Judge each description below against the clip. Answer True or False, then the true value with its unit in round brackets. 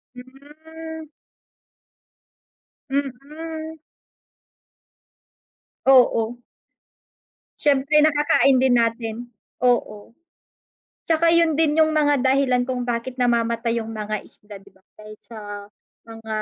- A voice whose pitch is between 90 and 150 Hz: False (260 Hz)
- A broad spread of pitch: False (4.7 semitones)